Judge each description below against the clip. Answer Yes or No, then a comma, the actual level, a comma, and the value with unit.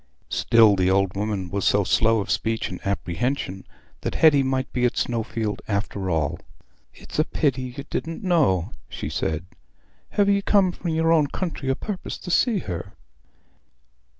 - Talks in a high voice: No, low, 115 Hz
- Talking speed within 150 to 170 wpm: Yes, average, 165 wpm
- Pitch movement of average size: No, wide, 8.4 semitones